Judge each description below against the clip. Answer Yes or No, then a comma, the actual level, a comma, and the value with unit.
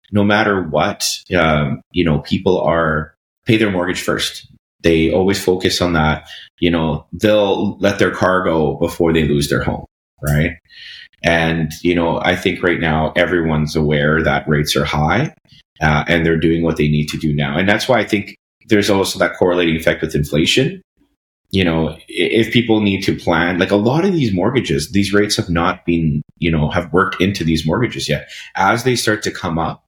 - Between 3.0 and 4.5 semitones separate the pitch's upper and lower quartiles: Yes, average, 4.2 semitones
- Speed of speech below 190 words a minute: No, average, 195 wpm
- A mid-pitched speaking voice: No, very low, 85 Hz